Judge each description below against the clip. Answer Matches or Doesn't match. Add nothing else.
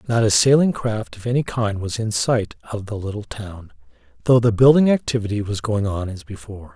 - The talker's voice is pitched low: Matches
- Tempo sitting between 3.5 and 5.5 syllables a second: Matches